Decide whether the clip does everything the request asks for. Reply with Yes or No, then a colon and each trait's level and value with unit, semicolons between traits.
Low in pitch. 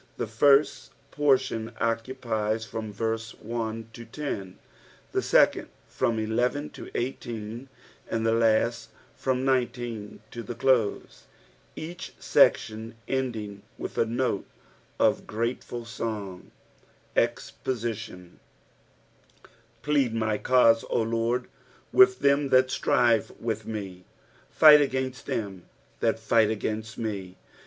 Yes: low, 115 Hz